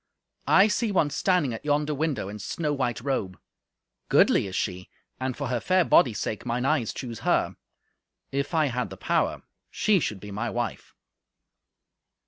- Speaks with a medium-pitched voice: No, low, 130 Hz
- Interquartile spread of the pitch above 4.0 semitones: Yes, average, 5.2 semitones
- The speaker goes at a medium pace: Yes, average, 165 wpm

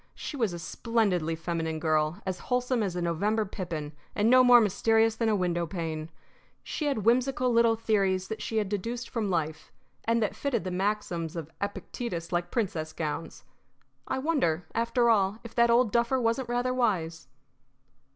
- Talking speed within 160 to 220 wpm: Yes, average, 170 wpm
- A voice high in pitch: Yes, high, 210 Hz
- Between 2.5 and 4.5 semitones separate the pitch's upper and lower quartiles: No, wide, 5.5 semitones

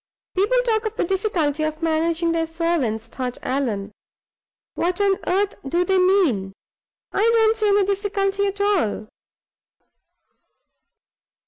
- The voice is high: Yes, very high, 360 Hz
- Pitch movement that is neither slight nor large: Yes, average, 4.7 semitones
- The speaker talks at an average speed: No, slow, 125 wpm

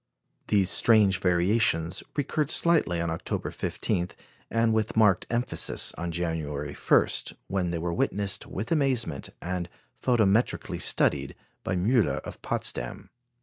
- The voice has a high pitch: No, very low, 95 Hz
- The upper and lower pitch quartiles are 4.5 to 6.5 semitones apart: Yes, average, 4.9 semitones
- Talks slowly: Yes, slow, 125 wpm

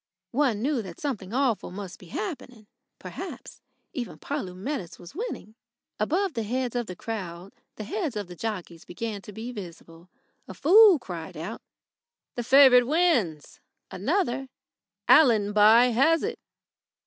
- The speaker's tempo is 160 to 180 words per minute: No, slow, 135 wpm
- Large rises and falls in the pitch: Yes, wide, 6.4 semitones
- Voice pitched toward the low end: No, high, 230 Hz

